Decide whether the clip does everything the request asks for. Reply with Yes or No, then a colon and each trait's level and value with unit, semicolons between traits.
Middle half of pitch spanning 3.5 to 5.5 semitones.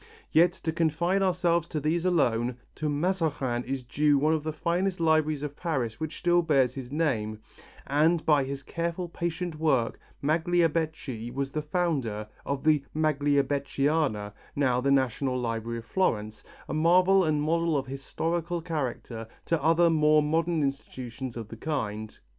Yes: average, 4.0 semitones